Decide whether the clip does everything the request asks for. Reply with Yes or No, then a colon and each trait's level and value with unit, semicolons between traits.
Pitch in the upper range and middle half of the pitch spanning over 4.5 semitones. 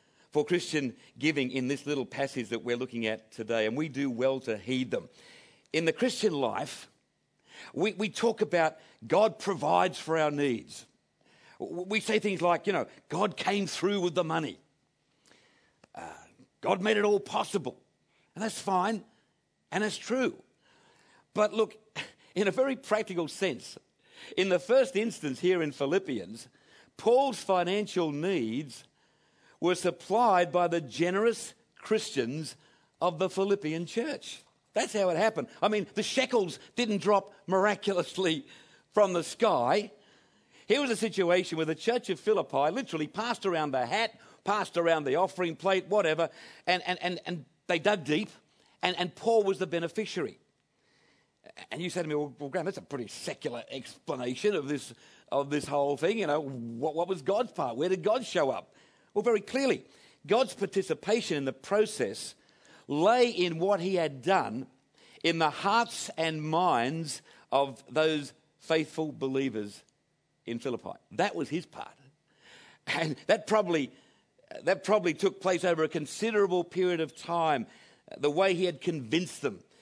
No: medium, 180 Hz; average, 5.1 semitones